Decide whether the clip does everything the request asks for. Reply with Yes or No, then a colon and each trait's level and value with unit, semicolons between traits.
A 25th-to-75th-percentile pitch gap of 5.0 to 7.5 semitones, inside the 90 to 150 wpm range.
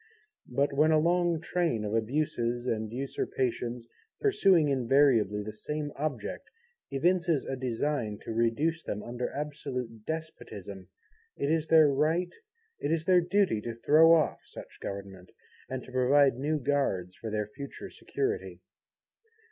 Yes: wide, 5.5 semitones; average, 140 wpm